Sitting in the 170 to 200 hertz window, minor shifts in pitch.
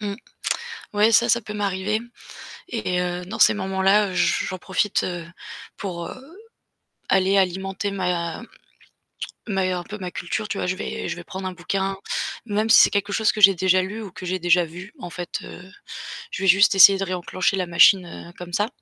Yes: high, 190 Hz; narrow, 2.2 semitones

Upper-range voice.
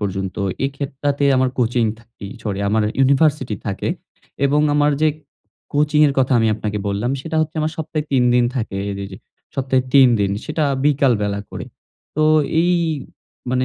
No: low, 130 Hz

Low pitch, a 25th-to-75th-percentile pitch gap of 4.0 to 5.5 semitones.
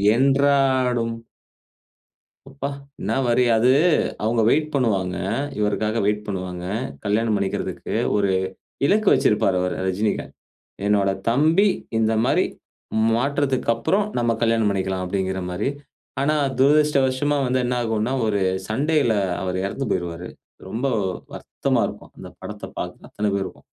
Yes: low, 115 Hz; average, 5.2 semitones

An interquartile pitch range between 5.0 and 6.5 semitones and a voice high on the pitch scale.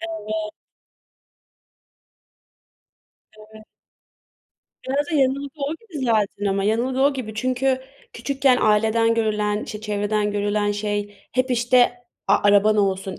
No: average, 3.8 semitones; high, 220 Hz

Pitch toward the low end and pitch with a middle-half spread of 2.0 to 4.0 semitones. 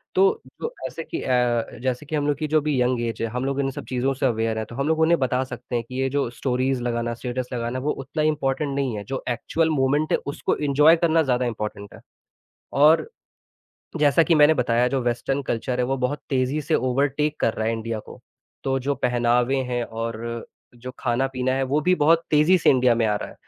Yes: low, 130 Hz; average, 3.3 semitones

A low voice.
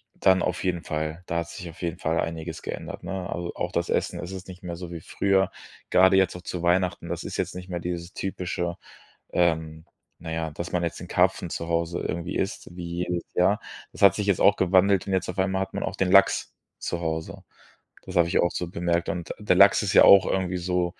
Yes: very low, 90 Hz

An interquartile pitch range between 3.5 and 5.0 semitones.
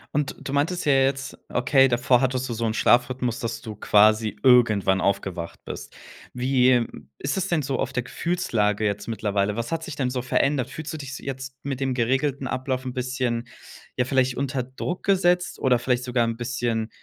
No: narrow, 2.6 semitones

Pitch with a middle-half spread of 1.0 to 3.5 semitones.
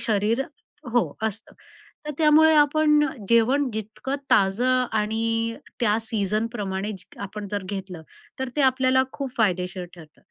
No: average, 4.3 semitones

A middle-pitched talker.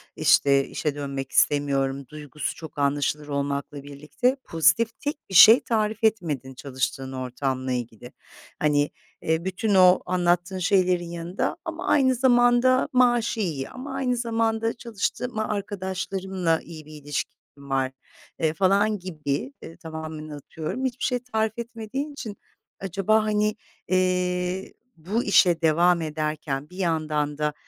Yes: medium, 175 Hz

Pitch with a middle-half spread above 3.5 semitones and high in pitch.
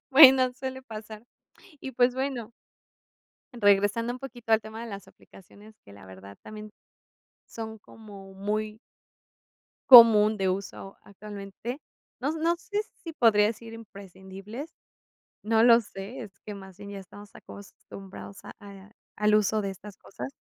No: average, 3.1 semitones; high, 215 Hz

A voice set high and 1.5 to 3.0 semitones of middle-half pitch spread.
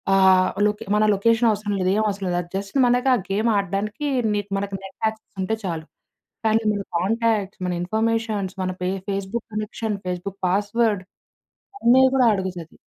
Yes: high, 205 Hz; average, 2.7 semitones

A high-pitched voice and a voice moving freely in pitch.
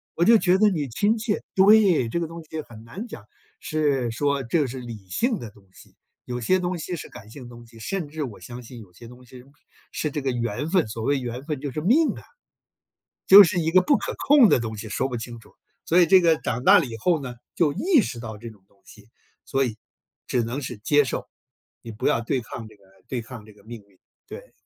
No: low, 130 Hz; wide, 6.8 semitones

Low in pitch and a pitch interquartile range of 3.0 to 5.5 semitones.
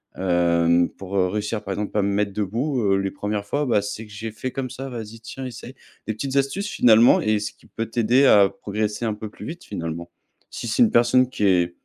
Yes: low, 105 Hz; average, 3.6 semitones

